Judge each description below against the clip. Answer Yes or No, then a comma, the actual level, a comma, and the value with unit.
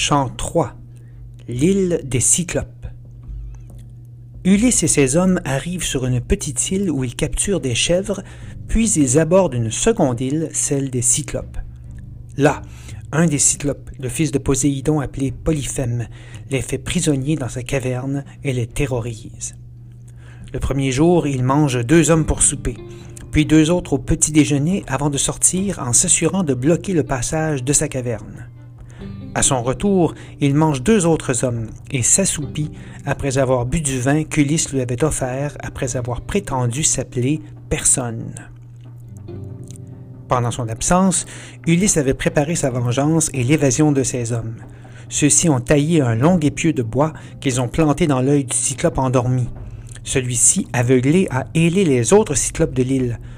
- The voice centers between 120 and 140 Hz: Yes, low, 135 Hz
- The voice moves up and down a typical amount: Yes, average, 4.4 semitones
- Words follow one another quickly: No, average, 150 wpm